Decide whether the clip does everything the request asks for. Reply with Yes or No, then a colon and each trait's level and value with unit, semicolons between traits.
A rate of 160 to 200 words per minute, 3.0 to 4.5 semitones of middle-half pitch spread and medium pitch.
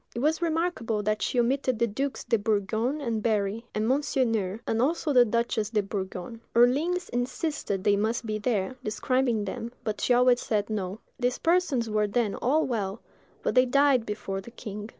No: average, 180 wpm; average, 3.5 semitones; high, 230 Hz